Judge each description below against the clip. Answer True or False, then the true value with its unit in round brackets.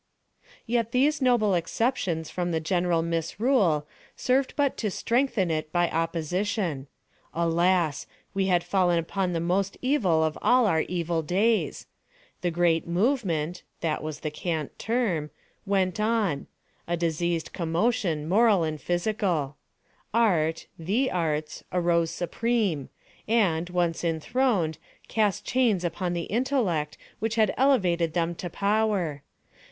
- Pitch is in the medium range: True (175 Hz)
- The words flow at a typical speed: False (120 wpm)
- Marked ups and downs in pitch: False (4.9 semitones)